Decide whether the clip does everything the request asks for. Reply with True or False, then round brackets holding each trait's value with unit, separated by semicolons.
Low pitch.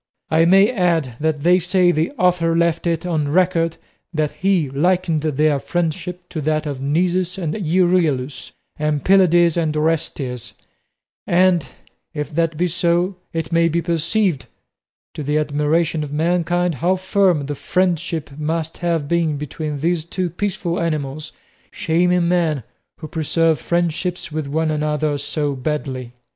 False (165 Hz)